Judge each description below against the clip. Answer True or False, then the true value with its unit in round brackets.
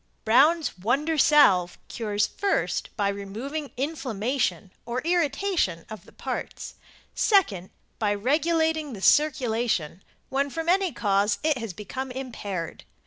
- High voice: True (255 Hz)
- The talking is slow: True (120 wpm)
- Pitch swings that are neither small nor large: False (7.0 semitones)